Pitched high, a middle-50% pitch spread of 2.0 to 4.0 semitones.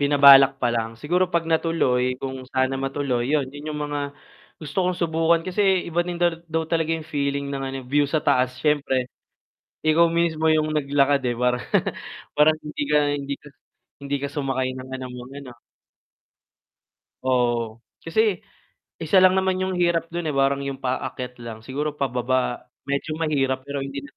No: medium, 140 Hz; average, 3.5 semitones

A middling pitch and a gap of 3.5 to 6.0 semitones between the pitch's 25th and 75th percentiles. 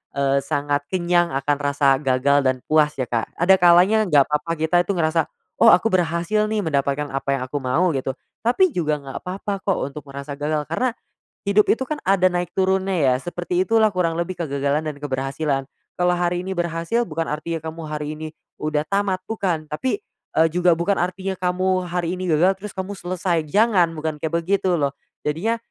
Yes: medium, 170 Hz; average, 4.1 semitones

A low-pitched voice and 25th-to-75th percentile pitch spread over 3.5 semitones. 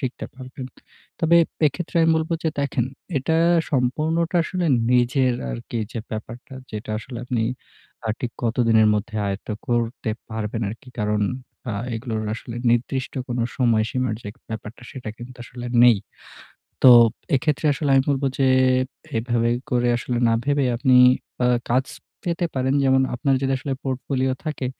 No: low, 125 Hz; average, 2.7 semitones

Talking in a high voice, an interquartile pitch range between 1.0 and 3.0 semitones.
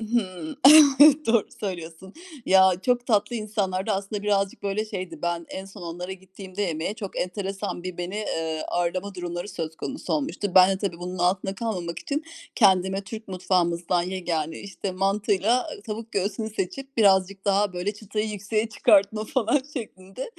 Yes: high, 195 Hz; average, 2.7 semitones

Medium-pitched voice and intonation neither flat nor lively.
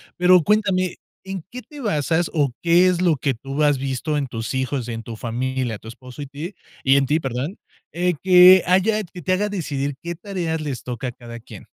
No: medium, 155 Hz; wide, 5.7 semitones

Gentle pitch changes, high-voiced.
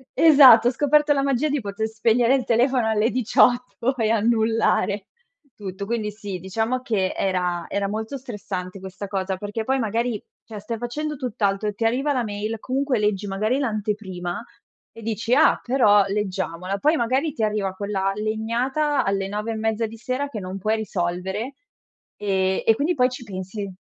No: average, 3.9 semitones; high, 220 Hz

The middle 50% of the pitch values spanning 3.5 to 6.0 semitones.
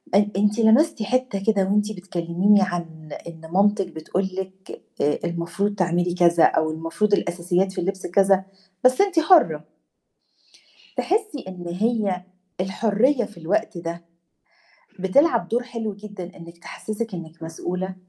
Yes: average, 3.8 semitones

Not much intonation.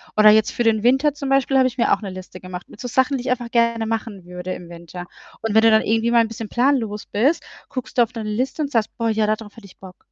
No: average, 3.1 semitones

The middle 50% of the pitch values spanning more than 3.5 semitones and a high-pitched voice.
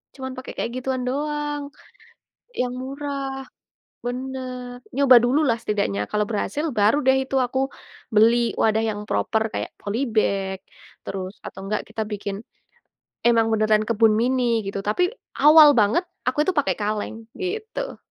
Yes: average, 4.3 semitones; high, 245 Hz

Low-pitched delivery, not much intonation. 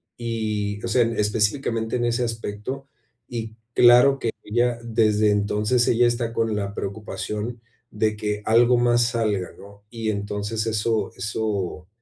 Yes: low, 110 Hz; narrow, 2.2 semitones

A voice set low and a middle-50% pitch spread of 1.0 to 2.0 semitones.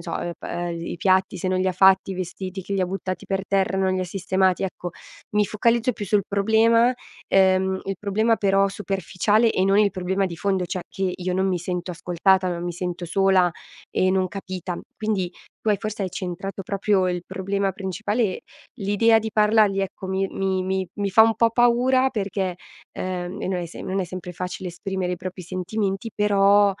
No: high, 190 Hz; narrow, 1.7 semitones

